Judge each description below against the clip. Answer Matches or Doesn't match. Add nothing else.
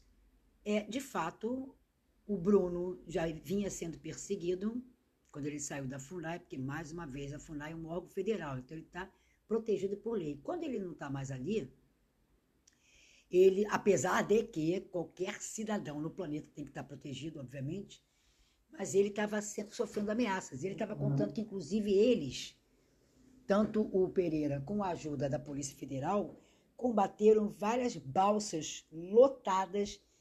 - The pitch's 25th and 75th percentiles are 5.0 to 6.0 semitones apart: Matches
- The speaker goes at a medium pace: Matches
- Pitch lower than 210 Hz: Matches